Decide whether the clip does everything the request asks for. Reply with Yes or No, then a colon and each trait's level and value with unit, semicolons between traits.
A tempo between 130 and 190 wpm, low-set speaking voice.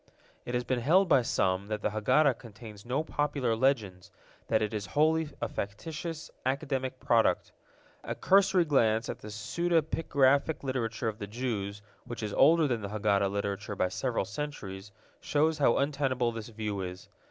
Yes: average, 165 wpm; low, 120 Hz